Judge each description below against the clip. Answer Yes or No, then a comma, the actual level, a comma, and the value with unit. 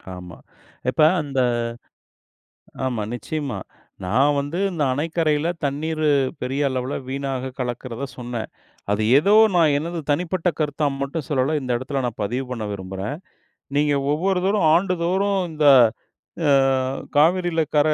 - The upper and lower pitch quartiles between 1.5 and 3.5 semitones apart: No, average, 4.2 semitones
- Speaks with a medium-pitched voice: Yes, medium, 145 Hz